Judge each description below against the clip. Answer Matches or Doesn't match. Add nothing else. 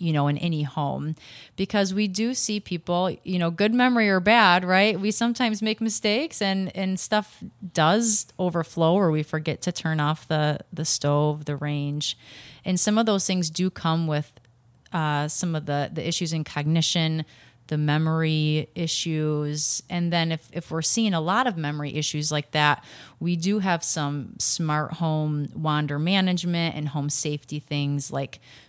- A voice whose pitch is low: Doesn't match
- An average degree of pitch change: Matches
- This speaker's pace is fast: Doesn't match